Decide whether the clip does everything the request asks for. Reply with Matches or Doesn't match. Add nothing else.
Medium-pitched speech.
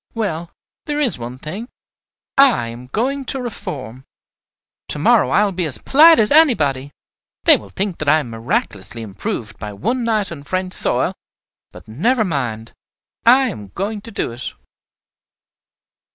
Matches